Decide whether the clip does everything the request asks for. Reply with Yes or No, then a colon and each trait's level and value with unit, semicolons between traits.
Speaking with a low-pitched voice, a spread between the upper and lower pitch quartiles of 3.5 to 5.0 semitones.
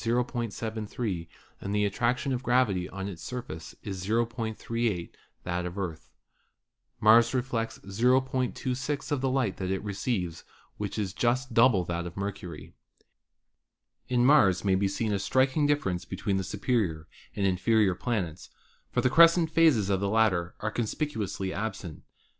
Yes: low, 105 Hz; average, 4.7 semitones